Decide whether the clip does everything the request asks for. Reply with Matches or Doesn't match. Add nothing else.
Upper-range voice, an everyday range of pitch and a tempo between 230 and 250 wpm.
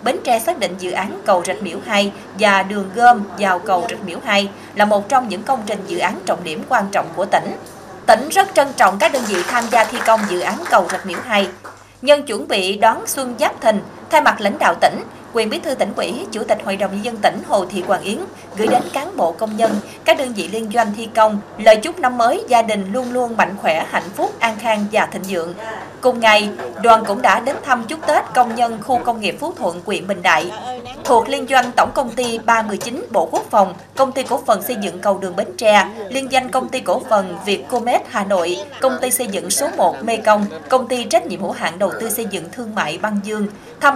Matches